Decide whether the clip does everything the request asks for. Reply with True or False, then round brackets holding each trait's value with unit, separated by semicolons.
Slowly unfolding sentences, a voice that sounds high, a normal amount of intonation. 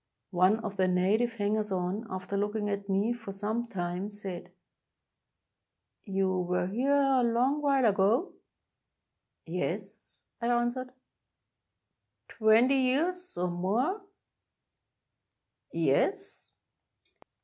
True (105 wpm; 215 Hz; 4.4 semitones)